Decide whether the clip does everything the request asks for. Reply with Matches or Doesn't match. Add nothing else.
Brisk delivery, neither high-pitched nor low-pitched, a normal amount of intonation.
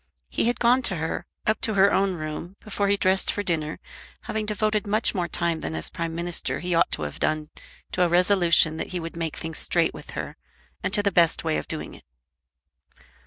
Matches